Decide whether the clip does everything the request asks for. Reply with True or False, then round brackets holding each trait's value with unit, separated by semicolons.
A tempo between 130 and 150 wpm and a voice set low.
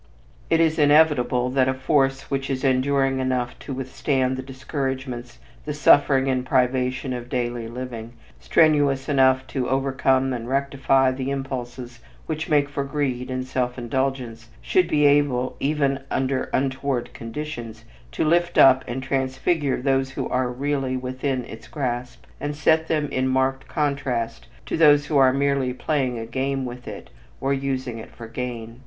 False (160 wpm; 130 Hz)